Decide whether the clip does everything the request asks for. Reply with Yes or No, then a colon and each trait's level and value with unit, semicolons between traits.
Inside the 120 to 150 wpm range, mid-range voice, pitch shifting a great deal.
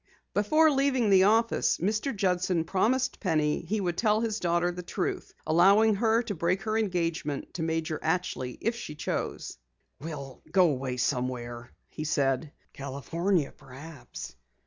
Yes: average, 145 wpm; medium, 175 Hz; wide, 6.0 semitones